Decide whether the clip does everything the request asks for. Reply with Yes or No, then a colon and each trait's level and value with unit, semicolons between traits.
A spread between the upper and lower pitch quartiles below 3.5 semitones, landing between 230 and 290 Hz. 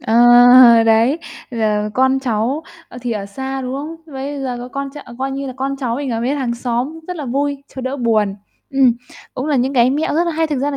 Yes: average, 2.8 semitones; very high, 260 Hz